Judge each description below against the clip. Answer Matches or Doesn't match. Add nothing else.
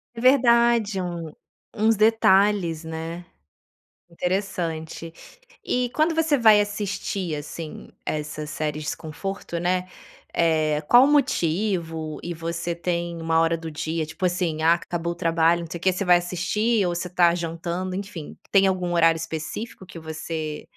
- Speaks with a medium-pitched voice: Matches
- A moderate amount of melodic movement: Matches